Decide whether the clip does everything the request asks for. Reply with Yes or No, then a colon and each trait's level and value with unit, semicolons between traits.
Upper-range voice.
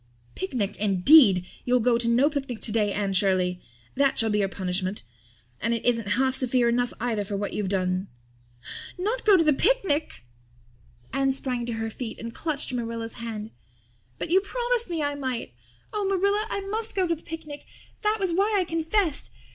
Yes: very high, 250 Hz